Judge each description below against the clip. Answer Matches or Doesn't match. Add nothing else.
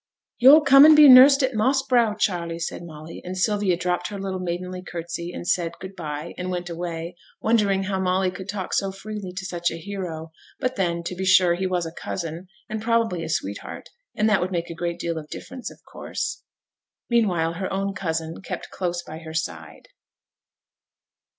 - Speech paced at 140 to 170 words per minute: Doesn't match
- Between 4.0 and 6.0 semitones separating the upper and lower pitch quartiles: Doesn't match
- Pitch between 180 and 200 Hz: Matches